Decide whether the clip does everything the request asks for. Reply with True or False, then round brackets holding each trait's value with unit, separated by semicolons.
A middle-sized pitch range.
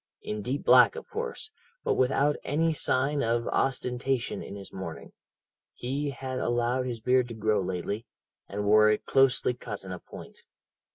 True (4.1 semitones)